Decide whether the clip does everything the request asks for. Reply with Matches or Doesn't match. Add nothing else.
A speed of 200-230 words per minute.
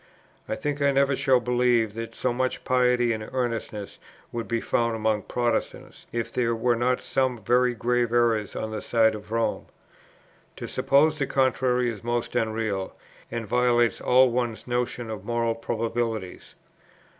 Doesn't match